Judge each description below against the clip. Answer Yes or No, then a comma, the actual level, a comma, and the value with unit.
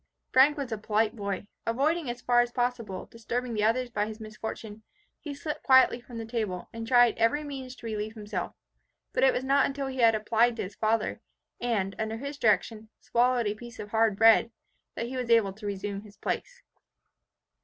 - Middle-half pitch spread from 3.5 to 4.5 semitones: No, average, 2.8 semitones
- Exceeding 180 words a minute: Yes, average, 195 wpm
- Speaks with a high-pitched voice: Yes, high, 230 Hz